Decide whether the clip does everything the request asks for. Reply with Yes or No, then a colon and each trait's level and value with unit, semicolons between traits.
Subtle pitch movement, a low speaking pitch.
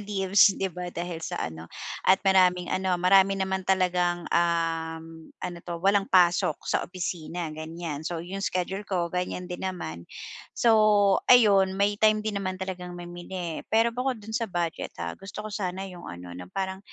No: narrow, 2.1 semitones; medium, 180 Hz